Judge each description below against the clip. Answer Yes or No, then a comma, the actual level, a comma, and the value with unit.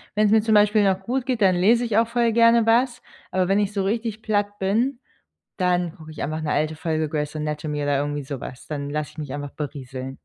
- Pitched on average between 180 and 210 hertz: Yes, medium, 185 Hz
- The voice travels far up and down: Yes, wide, 6.6 semitones